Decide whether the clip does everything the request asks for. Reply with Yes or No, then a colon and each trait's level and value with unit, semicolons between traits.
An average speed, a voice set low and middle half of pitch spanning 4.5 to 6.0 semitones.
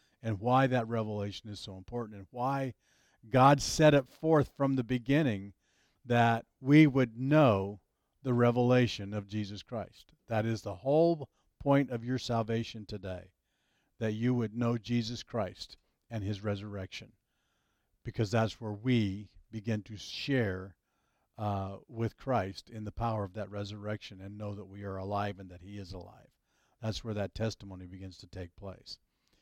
No: average, 160 wpm; low, 110 Hz; average, 3.4 semitones